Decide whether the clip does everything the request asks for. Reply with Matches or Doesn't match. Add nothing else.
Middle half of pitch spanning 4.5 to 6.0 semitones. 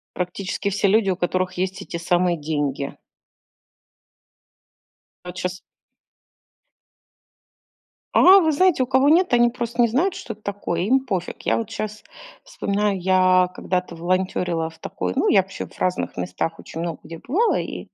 Matches